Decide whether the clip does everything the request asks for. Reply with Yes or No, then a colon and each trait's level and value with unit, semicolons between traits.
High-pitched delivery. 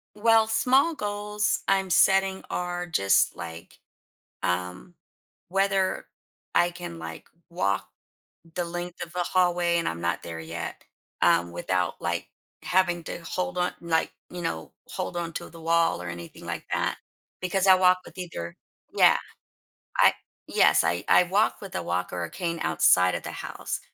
No: medium, 175 Hz